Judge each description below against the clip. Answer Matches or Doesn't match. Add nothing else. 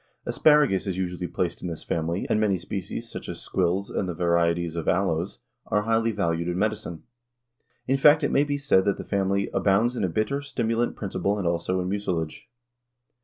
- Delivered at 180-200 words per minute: Matches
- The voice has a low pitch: Matches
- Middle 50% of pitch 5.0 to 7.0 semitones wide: Doesn't match